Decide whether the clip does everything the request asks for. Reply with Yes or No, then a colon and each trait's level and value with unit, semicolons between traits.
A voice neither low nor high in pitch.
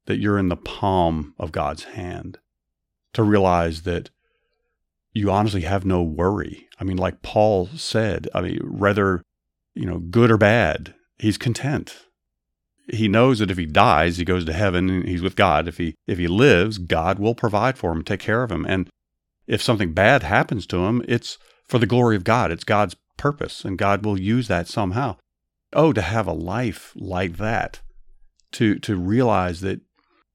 No: very low, 95 Hz